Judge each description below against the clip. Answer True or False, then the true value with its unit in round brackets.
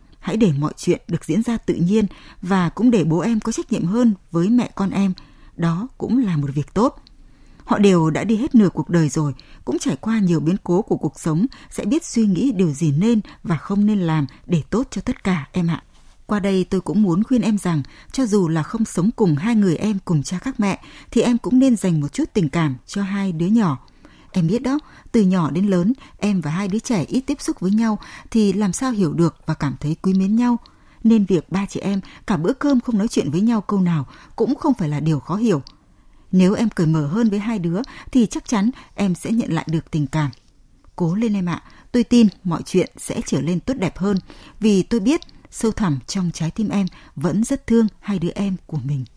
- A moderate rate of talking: True (240 wpm)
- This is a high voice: True (195 Hz)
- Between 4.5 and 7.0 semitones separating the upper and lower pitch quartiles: True (5.3 semitones)